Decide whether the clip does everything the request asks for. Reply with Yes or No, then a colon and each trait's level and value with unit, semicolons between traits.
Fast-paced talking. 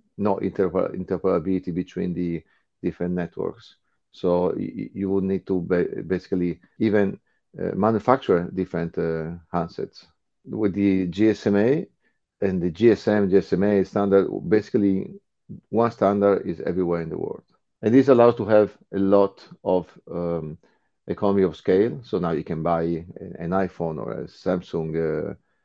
No: average, 140 wpm